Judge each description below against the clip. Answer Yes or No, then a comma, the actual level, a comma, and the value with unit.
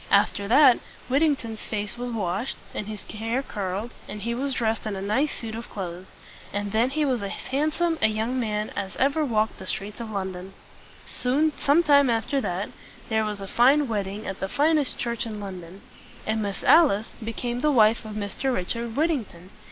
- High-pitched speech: Yes, high, 225 Hz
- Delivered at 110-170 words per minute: No, average, 185 wpm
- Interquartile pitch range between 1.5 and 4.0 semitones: No, average, 4.5 semitones